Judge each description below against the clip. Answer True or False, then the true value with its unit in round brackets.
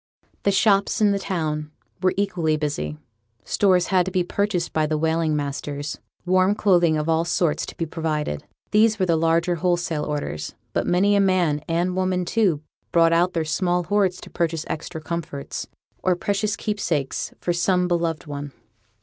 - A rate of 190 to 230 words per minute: False (170 wpm)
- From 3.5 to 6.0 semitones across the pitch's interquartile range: False (3.1 semitones)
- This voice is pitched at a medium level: True (170 Hz)